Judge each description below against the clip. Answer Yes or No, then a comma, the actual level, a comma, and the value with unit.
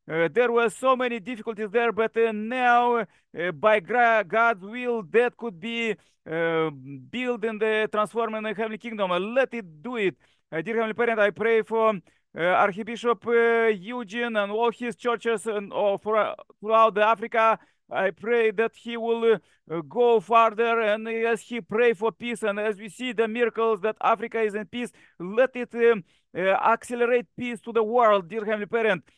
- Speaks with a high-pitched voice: Yes, high, 225 Hz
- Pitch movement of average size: No, narrow, 1.8 semitones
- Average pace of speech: Yes, average, 180 wpm